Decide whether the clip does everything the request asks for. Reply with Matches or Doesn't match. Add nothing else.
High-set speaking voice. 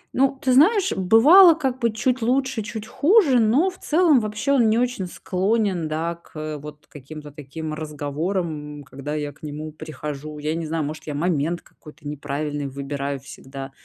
Doesn't match